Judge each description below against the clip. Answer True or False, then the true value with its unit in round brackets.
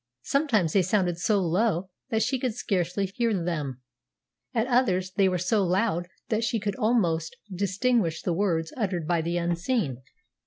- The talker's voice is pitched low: False (190 Hz)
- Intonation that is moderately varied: True (4.5 semitones)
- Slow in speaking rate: False (160 wpm)